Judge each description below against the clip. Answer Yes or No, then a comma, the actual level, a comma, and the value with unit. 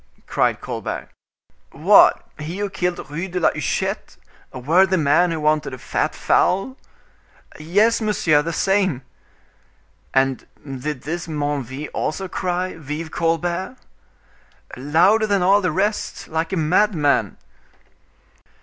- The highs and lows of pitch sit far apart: No, average, 4.1 semitones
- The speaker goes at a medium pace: No, slow, 120 wpm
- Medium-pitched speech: Yes, medium, 165 Hz